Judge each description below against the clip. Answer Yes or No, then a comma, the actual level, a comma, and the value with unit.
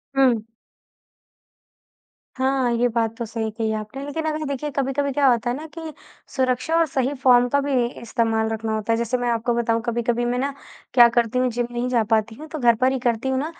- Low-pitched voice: No, high, 245 Hz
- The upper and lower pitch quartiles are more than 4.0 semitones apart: No, average, 2.8 semitones